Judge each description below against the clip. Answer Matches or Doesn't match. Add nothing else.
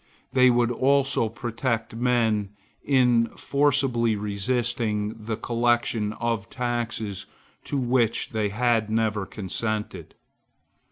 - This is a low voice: Matches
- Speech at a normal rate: Doesn't match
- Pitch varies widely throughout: Doesn't match